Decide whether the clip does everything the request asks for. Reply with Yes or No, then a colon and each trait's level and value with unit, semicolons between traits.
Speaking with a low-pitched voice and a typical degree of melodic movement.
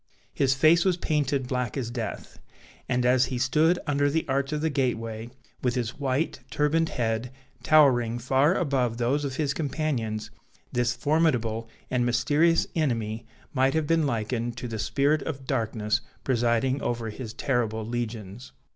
Yes: low, 130 Hz; average, 3.7 semitones